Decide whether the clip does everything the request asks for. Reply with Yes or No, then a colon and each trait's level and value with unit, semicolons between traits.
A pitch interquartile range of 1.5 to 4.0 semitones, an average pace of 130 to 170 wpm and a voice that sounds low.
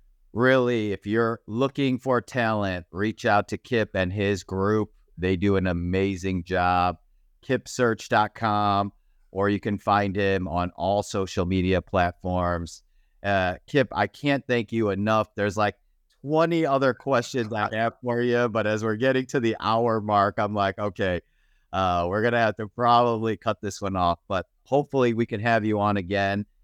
Yes: average, 3.4 semitones; average, 165 wpm; low, 105 Hz